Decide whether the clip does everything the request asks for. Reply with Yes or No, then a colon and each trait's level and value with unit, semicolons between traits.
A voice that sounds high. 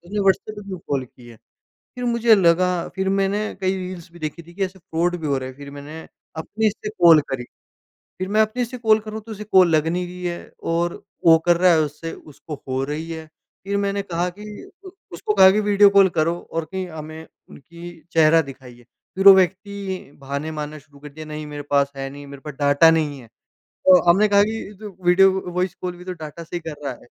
No: medium, 175 Hz